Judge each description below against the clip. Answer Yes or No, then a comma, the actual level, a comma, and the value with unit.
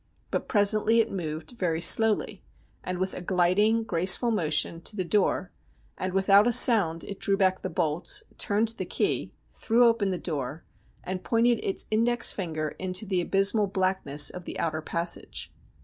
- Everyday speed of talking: Yes, average, 165 wpm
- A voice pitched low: No, high, 190 Hz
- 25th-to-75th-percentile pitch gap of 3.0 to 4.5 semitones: Yes, average, 3.9 semitones